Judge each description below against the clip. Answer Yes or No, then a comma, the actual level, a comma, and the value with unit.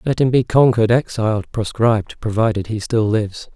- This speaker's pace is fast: No, average, 170 wpm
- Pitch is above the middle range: No, low, 115 Hz